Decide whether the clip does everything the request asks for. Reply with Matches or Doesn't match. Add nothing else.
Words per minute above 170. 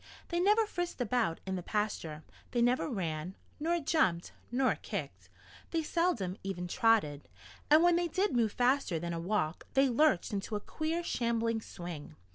Doesn't match